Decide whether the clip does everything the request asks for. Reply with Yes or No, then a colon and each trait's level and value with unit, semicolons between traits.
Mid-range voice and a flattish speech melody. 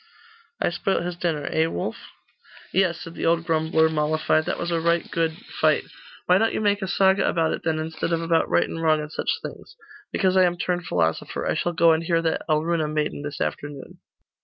Yes: medium, 165 Hz; narrow, 1.7 semitones